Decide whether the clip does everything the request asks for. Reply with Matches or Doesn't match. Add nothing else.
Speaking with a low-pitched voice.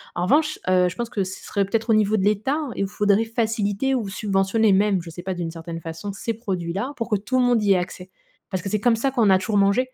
Doesn't match